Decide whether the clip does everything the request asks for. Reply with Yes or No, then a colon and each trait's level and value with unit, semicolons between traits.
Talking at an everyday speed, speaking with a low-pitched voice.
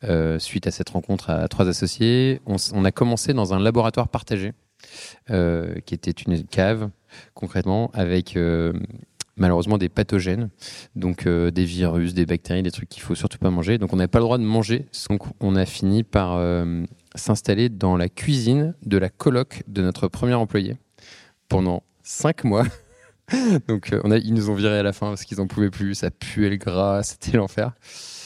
Yes: average, 200 wpm; low, 100 Hz